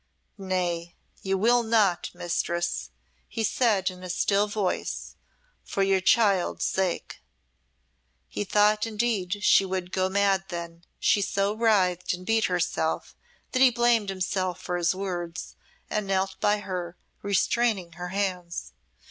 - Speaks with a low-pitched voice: No, high, 190 Hz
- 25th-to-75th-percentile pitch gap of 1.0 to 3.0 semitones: Yes, narrow, 2.6 semitones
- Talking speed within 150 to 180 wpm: No, slow, 135 wpm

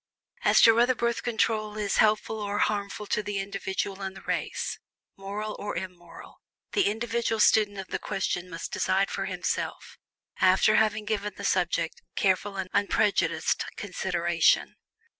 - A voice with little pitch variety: Yes, narrow, 2.1 semitones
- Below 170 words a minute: Yes, average, 145 wpm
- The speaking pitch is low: No, high, 205 Hz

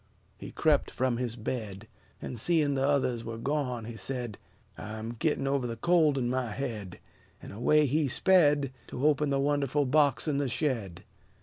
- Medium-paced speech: Yes, average, 170 wpm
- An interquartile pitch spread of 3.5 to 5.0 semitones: Yes, average, 3.8 semitones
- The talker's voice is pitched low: Yes, low, 130 Hz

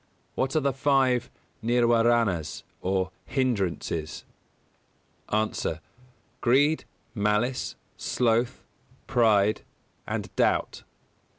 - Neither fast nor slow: No, slow, 75 wpm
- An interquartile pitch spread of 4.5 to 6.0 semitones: No, average, 3.7 semitones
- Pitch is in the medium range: No, low, 120 Hz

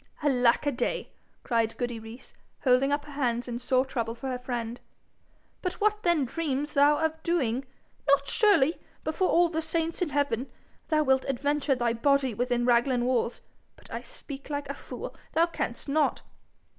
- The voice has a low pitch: No, very high, 275 Hz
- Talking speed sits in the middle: Yes, average, 170 wpm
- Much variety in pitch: No, average, 3.9 semitones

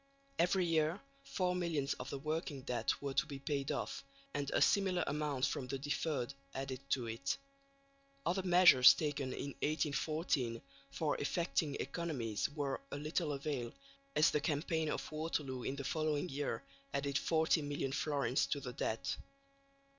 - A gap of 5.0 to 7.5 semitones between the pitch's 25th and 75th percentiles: No, average, 2.7 semitones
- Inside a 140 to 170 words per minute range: Yes, average, 155 wpm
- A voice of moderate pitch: Yes, medium, 145 Hz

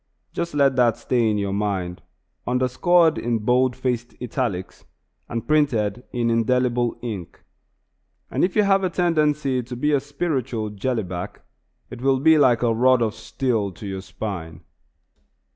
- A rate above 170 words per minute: No, average, 160 wpm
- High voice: No, low, 125 Hz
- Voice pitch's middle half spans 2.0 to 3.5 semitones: No, average, 4.1 semitones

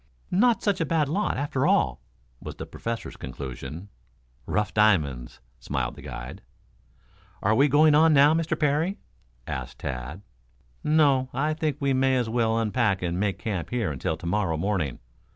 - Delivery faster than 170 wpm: No, average, 160 wpm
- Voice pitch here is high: No, low, 110 Hz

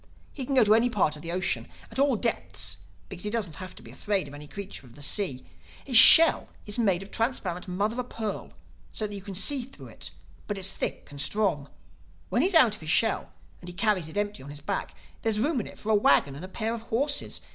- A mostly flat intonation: No, average, 5.2 semitones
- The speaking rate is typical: No, fast, 255 wpm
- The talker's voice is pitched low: No, high, 205 Hz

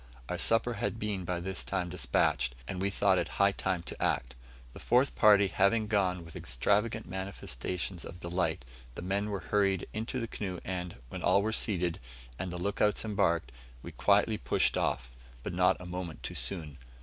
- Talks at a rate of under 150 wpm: No, average, 185 wpm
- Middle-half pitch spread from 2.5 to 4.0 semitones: Yes, average, 2.8 semitones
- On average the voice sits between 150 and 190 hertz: No, very low, 95 Hz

